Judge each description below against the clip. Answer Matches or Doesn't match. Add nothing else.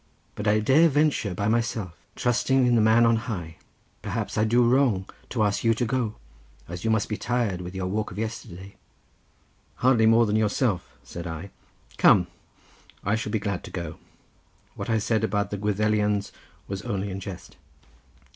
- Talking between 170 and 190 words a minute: Matches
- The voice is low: Matches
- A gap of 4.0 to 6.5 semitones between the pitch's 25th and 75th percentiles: Doesn't match